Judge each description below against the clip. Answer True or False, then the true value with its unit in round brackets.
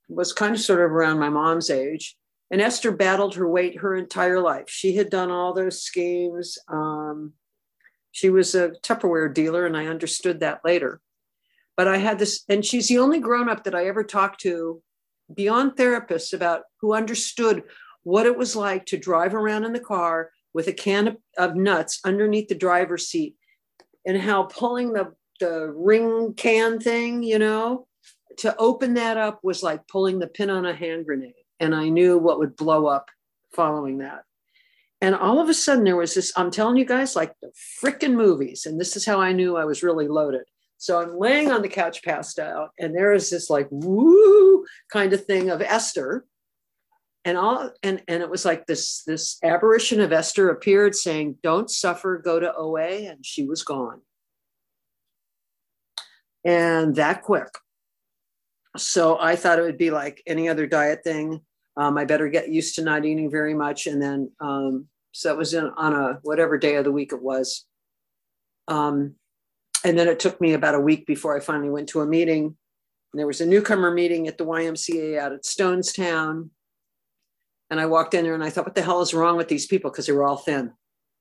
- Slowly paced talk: False (195 wpm)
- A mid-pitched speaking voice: True (175 Hz)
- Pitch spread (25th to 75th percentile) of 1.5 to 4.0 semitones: False (4.6 semitones)